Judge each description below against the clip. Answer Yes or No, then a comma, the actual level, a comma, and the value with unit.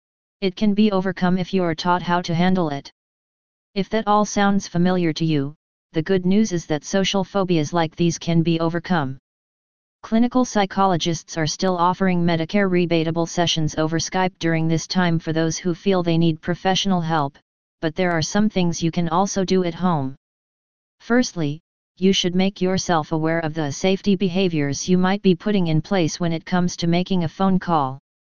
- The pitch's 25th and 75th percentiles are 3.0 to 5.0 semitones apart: No, narrow, 2.6 semitones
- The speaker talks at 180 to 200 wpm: Yes, average, 185 wpm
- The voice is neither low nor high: Yes, medium, 175 Hz